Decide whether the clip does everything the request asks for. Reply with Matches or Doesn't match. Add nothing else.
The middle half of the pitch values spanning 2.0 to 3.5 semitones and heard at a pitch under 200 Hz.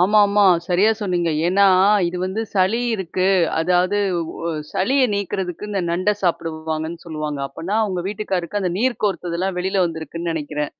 Matches